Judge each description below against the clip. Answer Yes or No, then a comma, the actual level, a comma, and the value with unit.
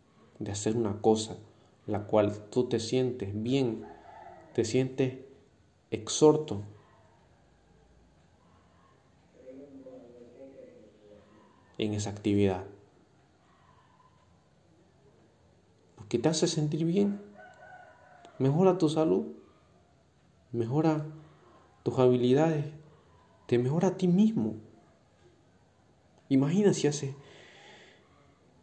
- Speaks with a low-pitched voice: Yes, low, 120 Hz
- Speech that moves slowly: Yes, slow, 75 wpm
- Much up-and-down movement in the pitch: Yes, wide, 6.2 semitones